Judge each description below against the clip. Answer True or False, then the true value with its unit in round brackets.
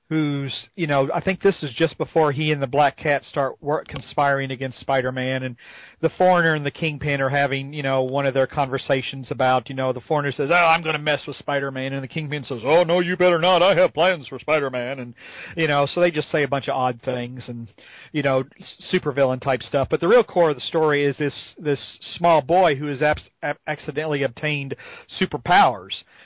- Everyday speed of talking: False (230 wpm)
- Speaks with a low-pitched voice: False (145 Hz)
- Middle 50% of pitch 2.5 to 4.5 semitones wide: True (3.0 semitones)